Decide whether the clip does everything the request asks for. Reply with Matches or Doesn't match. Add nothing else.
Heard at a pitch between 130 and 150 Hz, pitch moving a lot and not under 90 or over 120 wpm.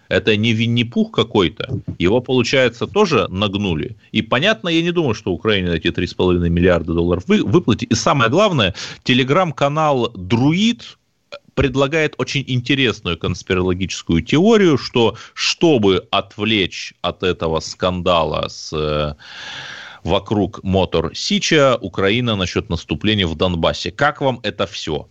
Doesn't match